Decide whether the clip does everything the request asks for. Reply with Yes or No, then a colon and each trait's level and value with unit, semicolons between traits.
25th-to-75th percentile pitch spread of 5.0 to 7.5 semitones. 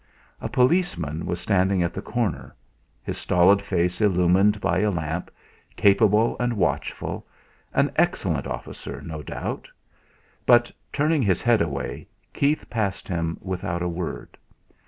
No: average, 4.4 semitones